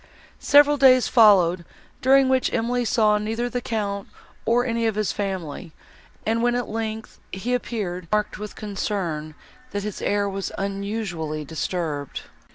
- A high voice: Yes, high, 210 Hz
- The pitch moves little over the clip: No, average, 3.7 semitones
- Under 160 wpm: Yes, average, 150 wpm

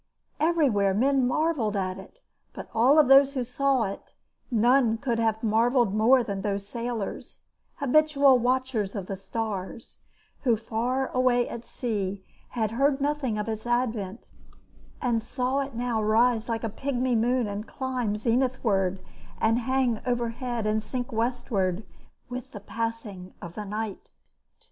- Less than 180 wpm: Yes, average, 145 wpm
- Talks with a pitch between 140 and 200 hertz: No, high, 235 Hz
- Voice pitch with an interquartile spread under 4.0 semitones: Yes, average, 3.2 semitones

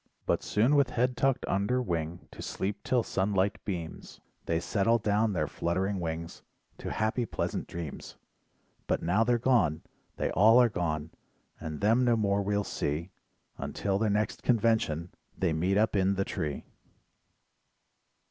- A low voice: Yes, low, 100 Hz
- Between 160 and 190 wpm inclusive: No, average, 150 wpm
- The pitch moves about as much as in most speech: Yes, average, 4.8 semitones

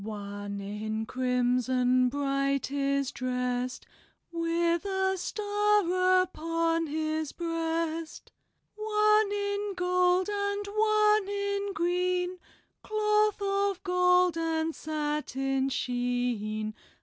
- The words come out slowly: Yes, slow, 90 wpm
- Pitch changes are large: Yes, wide, 7.4 semitones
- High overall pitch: Yes, very high, 330 Hz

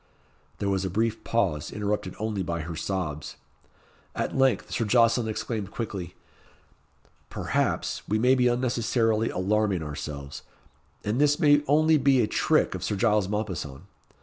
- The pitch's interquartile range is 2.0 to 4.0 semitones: No, average, 4.4 semitones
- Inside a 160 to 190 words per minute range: No, average, 145 wpm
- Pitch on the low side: Yes, low, 105 Hz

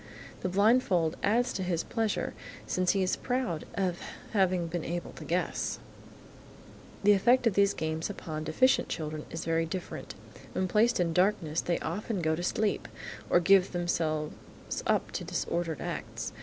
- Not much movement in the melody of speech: No, average, 3.6 semitones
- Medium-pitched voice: Yes, medium, 180 Hz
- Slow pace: No, average, 155 wpm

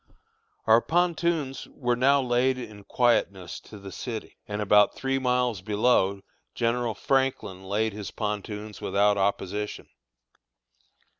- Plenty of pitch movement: No, average, 3.7 semitones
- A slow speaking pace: Yes, slow, 120 wpm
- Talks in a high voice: No, low, 110 Hz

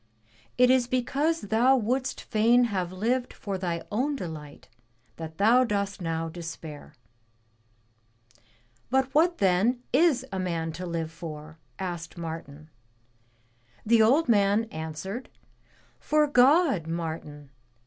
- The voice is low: No, high, 200 Hz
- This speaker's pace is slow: Yes, slow, 120 wpm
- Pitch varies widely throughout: Yes, wide, 7.3 semitones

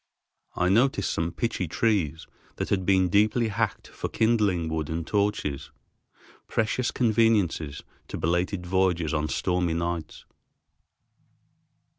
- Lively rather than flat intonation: No, average, 4.4 semitones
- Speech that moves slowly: Yes, slow, 115 wpm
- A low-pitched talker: Yes, very low, 90 Hz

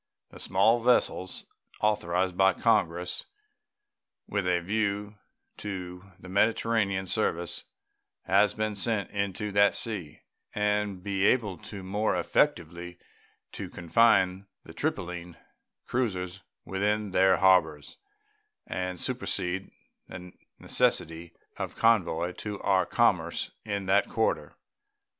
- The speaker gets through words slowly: Yes, slow, 105 wpm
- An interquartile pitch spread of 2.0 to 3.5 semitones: Yes, average, 2.7 semitones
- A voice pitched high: No, very low, 95 Hz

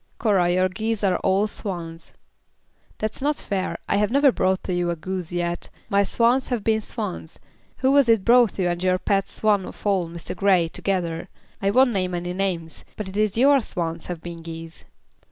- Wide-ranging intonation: No, average, 3.7 semitones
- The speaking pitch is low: No, high, 190 Hz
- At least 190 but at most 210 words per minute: Yes, average, 195 wpm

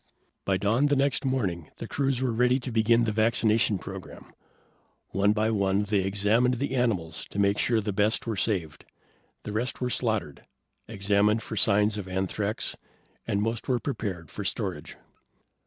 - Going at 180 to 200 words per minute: No, average, 165 wpm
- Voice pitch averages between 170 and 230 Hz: No, low, 105 Hz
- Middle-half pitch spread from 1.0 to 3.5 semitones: Yes, average, 3.0 semitones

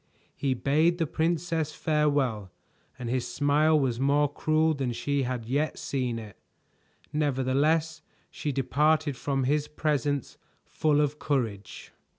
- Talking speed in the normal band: No, slow, 130 wpm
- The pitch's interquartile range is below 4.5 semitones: Yes, average, 2.9 semitones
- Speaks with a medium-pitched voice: Yes, medium, 145 Hz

